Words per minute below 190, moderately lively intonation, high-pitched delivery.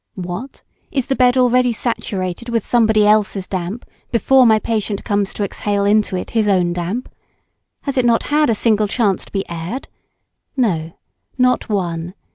Yes: average, 165 wpm; average, 4.3 semitones; high, 215 Hz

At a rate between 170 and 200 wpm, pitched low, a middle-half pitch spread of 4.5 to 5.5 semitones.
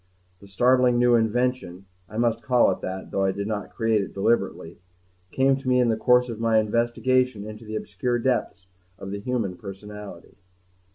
No: average, 180 wpm; low, 110 Hz; average, 3.6 semitones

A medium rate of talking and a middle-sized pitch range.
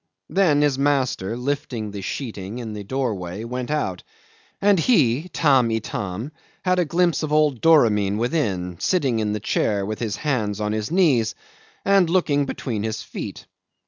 No: average, 160 wpm; wide, 6.1 semitones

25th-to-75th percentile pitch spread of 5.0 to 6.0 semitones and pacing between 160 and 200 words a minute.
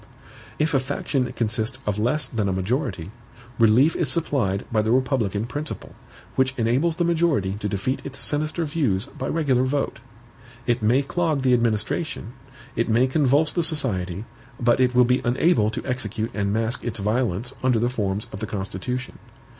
No: average, 4.4 semitones; average, 170 wpm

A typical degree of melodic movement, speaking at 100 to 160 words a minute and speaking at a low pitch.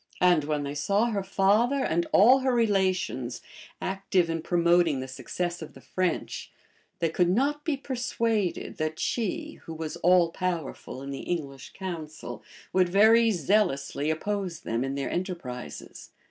No: average, 5.0 semitones; average, 150 wpm; medium, 175 Hz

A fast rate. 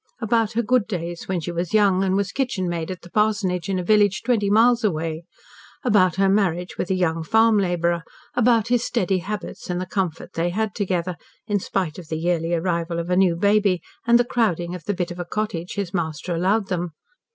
Yes: fast, 210 wpm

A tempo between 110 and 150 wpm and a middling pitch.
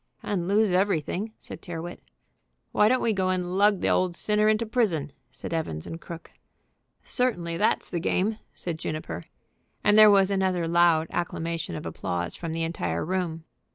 No: average, 165 wpm; medium, 175 Hz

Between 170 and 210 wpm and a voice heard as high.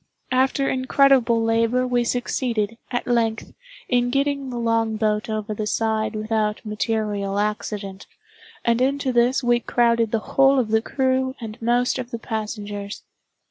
No: average, 140 wpm; high, 230 Hz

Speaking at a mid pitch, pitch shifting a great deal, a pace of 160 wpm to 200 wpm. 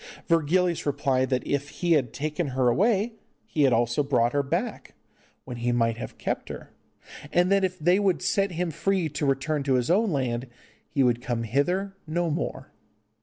Yes: medium, 150 Hz; wide, 5.7 semitones; average, 185 wpm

